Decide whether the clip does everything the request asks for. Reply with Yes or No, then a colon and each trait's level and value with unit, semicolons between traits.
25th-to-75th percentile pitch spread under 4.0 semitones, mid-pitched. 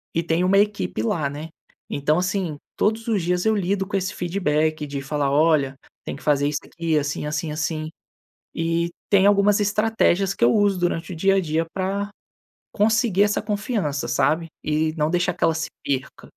No: average, 4.7 semitones; medium, 170 Hz